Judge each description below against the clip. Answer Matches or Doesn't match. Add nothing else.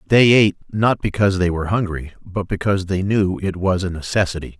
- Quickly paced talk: Doesn't match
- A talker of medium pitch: Doesn't match